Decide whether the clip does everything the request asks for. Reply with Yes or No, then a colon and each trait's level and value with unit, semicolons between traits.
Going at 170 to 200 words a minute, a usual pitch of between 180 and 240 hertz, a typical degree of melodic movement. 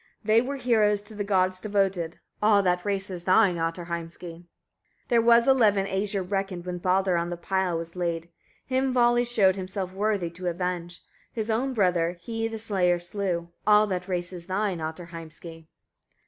Yes: average, 175 wpm; high, 190 Hz; average, 3.2 semitones